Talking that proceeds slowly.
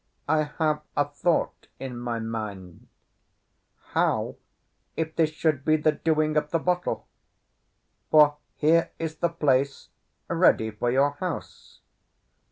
Yes: slow, 125 wpm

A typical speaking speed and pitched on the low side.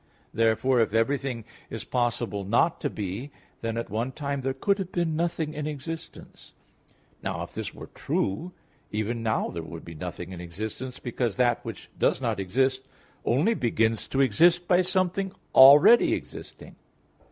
Yes: average, 160 wpm; low, 125 Hz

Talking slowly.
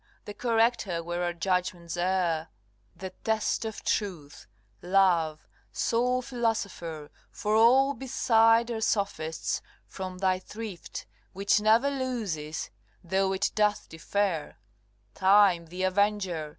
Yes: slow, 110 wpm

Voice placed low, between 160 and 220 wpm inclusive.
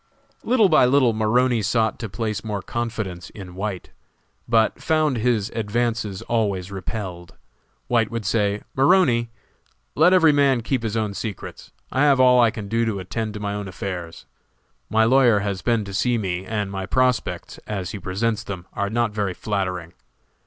Yes: low, 110 Hz; average, 170 wpm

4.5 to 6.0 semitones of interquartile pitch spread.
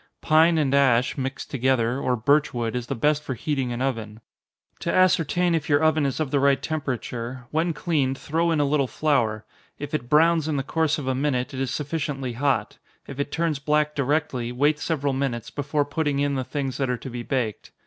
No: average, 3.0 semitones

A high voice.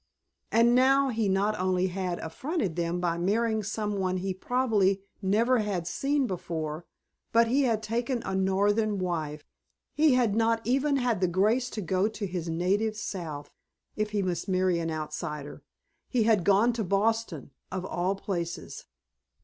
Yes: high, 200 Hz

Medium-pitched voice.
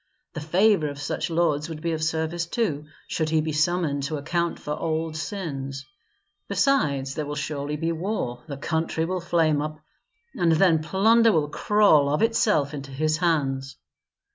Yes: medium, 155 Hz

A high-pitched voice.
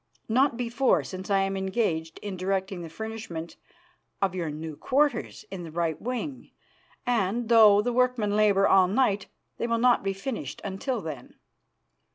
Yes: high, 200 Hz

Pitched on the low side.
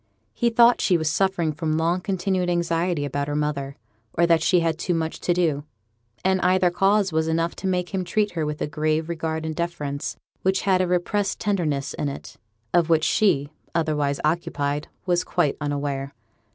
No: medium, 165 Hz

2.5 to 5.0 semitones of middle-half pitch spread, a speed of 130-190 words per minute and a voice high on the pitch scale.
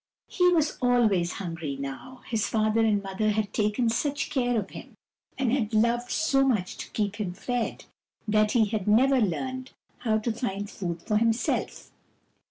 Yes: average, 3.3 semitones; average, 170 wpm; high, 220 Hz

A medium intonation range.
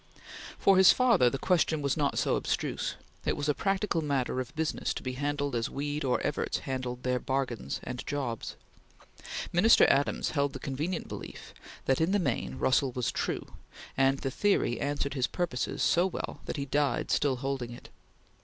Yes: average, 3.5 semitones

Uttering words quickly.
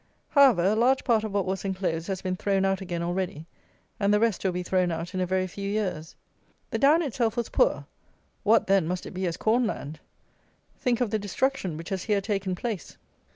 Yes: fast, 215 wpm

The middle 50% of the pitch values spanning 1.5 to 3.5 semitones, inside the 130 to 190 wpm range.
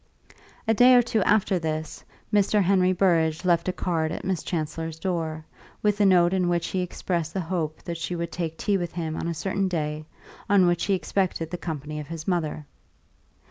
No: average, 2.9 semitones; average, 200 wpm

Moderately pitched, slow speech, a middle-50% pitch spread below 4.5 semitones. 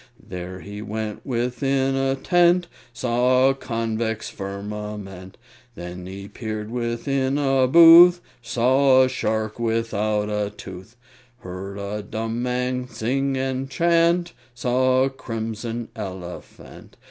No: low, 115 Hz; slow, 115 wpm; average, 4.0 semitones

